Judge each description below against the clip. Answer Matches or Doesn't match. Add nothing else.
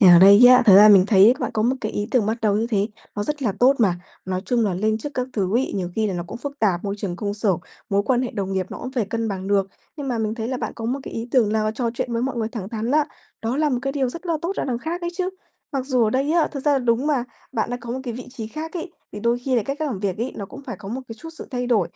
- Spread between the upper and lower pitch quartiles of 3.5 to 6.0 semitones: Matches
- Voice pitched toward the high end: Matches